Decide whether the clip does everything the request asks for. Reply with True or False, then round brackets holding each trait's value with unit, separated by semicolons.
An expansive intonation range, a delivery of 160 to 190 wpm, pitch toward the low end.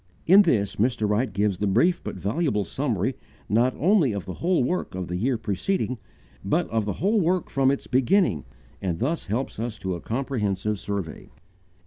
True (6.7 semitones; 180 wpm; 115 Hz)